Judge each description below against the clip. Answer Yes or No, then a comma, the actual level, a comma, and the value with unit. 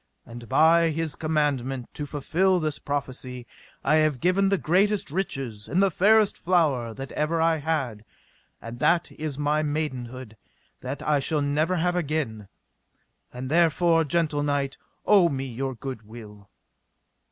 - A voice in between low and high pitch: Yes, medium, 150 Hz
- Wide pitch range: No, average, 4.2 semitones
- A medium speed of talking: Yes, average, 145 wpm